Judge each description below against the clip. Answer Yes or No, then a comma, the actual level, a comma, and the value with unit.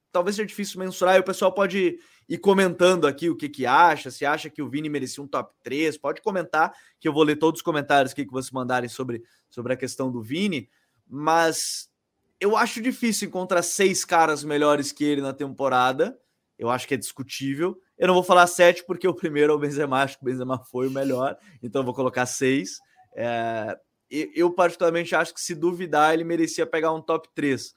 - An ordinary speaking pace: No, fast, 205 wpm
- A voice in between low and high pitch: Yes, medium, 155 Hz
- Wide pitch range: No, average, 4.8 semitones